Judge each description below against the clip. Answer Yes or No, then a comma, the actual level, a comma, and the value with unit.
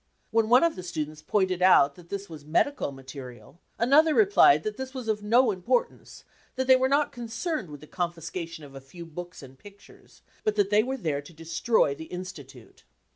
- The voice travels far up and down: Yes, wide, 7.3 semitones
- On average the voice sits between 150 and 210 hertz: Yes, medium, 185 Hz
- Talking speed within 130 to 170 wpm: No, average, 195 wpm